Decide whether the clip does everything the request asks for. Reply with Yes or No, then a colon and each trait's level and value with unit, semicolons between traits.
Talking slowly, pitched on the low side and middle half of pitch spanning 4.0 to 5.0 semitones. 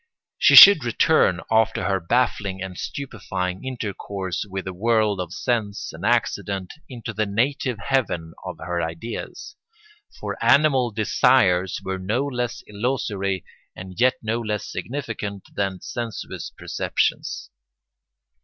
Yes: slow, 125 wpm; low, 105 Hz; average, 4.3 semitones